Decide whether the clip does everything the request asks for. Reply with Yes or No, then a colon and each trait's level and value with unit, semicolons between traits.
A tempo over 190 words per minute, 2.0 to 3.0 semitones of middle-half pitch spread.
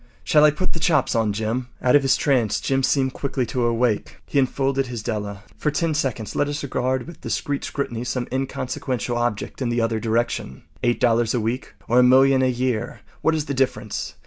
Yes: average, 200 wpm; average, 2.7 semitones